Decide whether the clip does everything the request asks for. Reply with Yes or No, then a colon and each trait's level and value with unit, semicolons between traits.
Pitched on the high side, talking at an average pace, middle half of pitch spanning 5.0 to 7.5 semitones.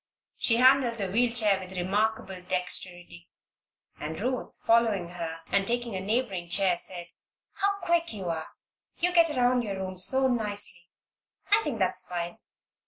Yes: high, 200 Hz; average, 155 wpm; average, 5.3 semitones